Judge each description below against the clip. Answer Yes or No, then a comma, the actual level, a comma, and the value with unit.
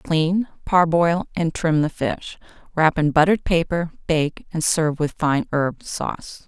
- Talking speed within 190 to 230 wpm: No, average, 160 wpm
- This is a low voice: No, medium, 160 Hz